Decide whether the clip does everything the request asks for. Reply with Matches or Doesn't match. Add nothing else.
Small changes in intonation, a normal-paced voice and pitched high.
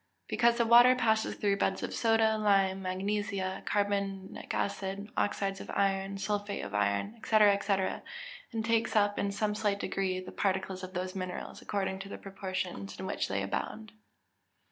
Matches